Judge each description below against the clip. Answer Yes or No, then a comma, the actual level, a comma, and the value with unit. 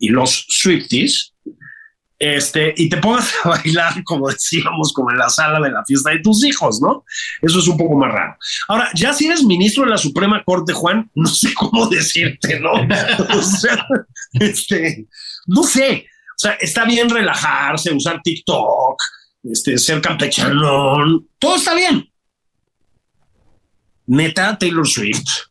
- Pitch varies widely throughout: Yes, wide, 7.3 semitones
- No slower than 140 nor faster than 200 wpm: Yes, average, 150 wpm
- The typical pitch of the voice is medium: Yes, medium, 180 Hz